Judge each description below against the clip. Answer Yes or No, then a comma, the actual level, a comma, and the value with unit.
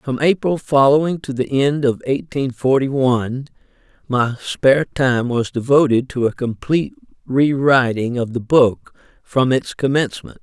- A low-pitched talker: Yes, low, 130 Hz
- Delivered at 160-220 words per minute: No, average, 145 wpm